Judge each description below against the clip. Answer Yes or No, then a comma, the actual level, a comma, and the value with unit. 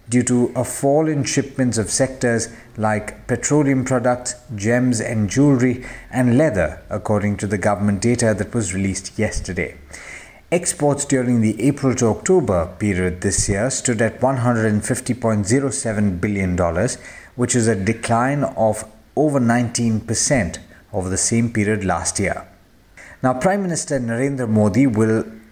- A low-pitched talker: Yes, low, 115 Hz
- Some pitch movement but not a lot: Yes, average, 3.3 semitones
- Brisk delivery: No, slow, 135 wpm